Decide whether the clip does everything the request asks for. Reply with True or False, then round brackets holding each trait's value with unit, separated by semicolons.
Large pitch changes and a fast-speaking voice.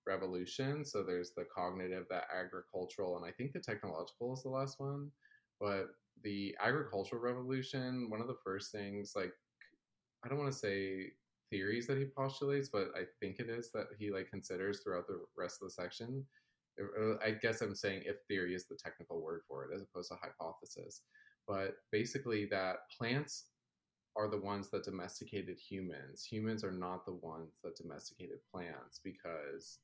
False (5.8 semitones; 170 wpm)